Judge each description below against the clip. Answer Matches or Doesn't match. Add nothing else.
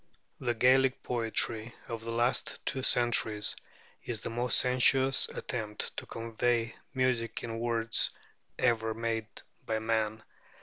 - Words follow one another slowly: Matches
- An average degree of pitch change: Doesn't match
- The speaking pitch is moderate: Doesn't match